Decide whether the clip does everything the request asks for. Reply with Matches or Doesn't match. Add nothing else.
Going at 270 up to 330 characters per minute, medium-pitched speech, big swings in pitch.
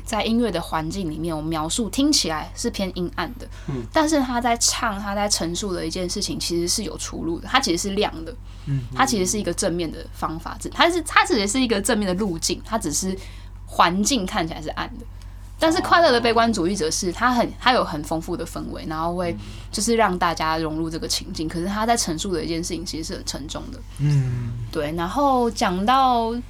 Matches